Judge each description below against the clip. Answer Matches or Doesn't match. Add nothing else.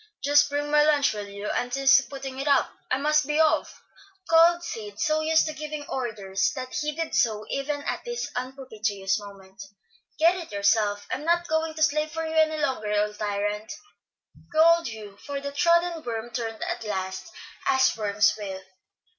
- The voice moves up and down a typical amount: Doesn't match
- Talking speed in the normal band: Matches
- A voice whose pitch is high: Matches